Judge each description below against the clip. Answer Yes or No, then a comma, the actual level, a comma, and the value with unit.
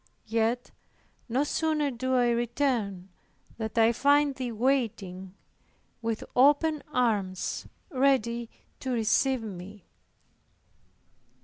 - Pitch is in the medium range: No, high, 240 Hz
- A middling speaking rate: No, slow, 95 wpm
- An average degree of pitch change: Yes, average, 3.6 semitones